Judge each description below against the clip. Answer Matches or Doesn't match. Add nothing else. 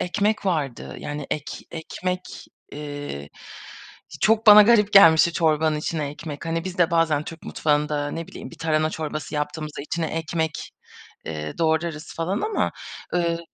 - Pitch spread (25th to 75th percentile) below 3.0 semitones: Matches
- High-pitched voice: Doesn't match